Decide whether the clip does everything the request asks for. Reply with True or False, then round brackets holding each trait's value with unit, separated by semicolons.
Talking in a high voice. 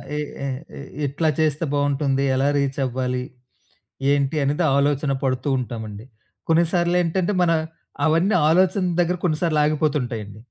False (145 Hz)